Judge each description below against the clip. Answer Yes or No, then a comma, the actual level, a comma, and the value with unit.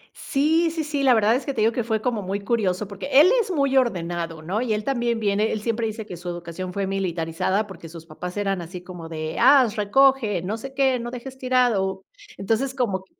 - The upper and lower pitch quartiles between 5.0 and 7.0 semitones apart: Yes, wide, 5.5 semitones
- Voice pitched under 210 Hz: No, high, 215 Hz